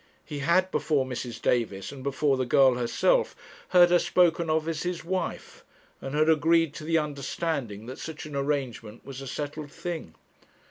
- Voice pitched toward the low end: No, medium, 150 Hz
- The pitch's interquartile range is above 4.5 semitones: No, average, 3.9 semitones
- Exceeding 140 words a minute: Yes, average, 175 wpm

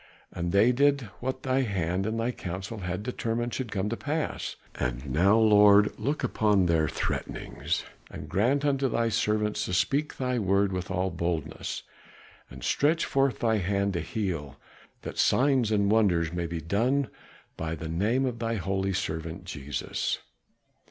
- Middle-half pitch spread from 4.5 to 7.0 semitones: Yes, wide, 5.4 semitones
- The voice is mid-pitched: No, low, 105 Hz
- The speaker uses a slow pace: No, average, 160 wpm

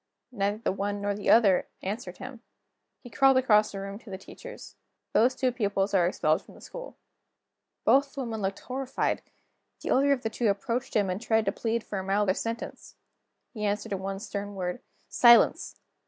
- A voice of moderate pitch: No, high, 210 Hz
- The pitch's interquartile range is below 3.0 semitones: No, average, 3.7 semitones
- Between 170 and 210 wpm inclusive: Yes, average, 185 wpm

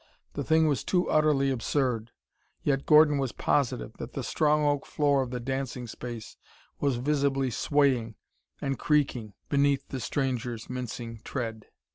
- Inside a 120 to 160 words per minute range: Yes, average, 145 wpm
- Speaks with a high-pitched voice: No, low, 135 Hz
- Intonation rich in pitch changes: No, average, 3.1 semitones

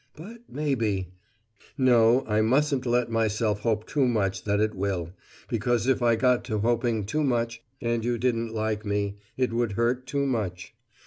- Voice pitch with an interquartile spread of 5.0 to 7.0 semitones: No, average, 2.9 semitones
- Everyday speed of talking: Yes, average, 170 wpm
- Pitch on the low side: Yes, low, 115 Hz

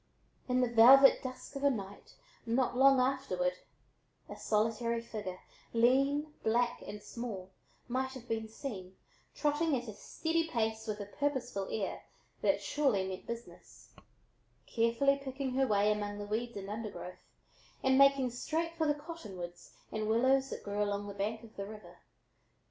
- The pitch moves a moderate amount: Yes, average, 4.6 semitones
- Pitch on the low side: No, high, 235 Hz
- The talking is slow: No, average, 155 wpm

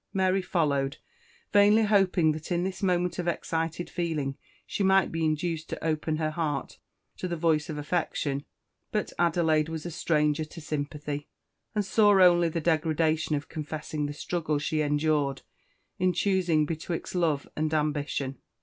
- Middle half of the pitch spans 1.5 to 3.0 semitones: Yes, narrow, 2.6 semitones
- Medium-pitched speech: Yes, medium, 160 Hz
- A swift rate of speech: No, average, 155 wpm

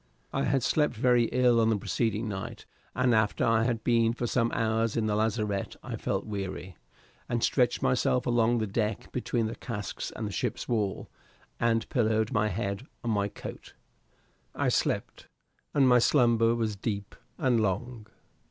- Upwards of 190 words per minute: No, average, 170 wpm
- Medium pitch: No, low, 115 Hz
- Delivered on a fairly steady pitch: Yes, narrow, 2.2 semitones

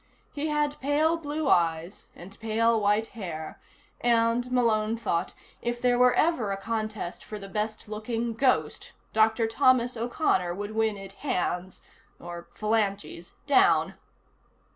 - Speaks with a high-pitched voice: Yes, high, 225 Hz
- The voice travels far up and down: No, average, 3.7 semitones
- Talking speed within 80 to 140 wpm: Yes, slow, 135 wpm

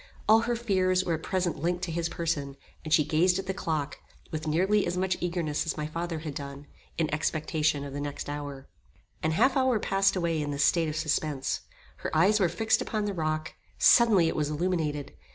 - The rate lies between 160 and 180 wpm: No, fast, 205 wpm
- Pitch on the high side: No, medium, 165 Hz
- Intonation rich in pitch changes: No, average, 3.5 semitones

